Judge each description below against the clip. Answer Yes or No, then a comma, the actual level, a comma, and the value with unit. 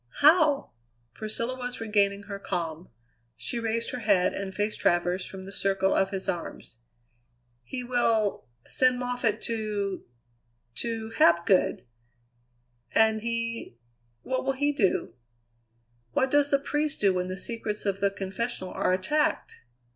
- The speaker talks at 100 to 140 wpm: Yes, slow, 135 wpm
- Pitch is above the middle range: Yes, high, 215 Hz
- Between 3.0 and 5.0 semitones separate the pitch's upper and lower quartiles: Yes, average, 4.2 semitones